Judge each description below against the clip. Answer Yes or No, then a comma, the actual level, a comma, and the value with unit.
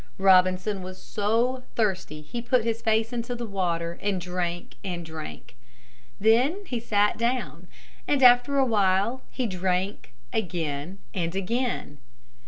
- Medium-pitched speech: No, high, 205 Hz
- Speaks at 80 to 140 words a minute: Yes, slow, 135 wpm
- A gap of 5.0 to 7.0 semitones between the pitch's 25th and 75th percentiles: No, average, 4.5 semitones